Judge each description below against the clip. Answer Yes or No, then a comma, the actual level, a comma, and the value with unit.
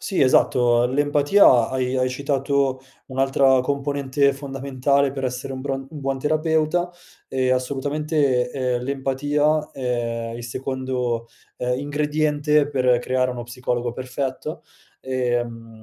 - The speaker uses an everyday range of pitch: No, narrow, 2.2 semitones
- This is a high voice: No, low, 135 Hz